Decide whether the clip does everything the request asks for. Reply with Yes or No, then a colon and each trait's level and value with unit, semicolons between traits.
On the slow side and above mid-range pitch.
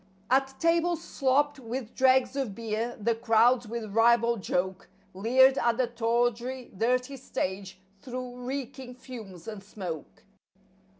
Yes: slow, 125 wpm; high, 240 Hz